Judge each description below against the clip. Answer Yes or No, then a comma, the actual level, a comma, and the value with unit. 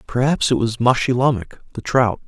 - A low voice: Yes, low, 125 Hz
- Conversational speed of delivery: Yes, average, 160 wpm